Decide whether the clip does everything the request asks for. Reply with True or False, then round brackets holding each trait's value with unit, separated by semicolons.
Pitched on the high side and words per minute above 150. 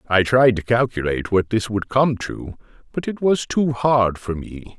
False (115 Hz; 200 wpm)